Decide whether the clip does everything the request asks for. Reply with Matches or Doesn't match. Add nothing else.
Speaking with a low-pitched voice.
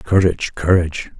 Matches